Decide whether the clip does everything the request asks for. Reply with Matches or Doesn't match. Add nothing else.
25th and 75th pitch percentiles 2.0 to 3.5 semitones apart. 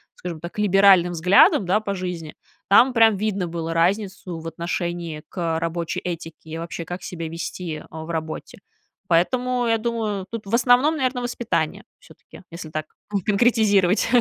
Doesn't match